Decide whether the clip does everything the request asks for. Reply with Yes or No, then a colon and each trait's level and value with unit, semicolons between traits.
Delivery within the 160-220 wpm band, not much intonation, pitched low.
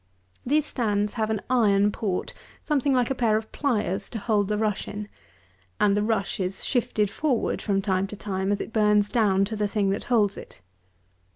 No: average, 195 wpm; narrow, 2.3 semitones; high, 210 Hz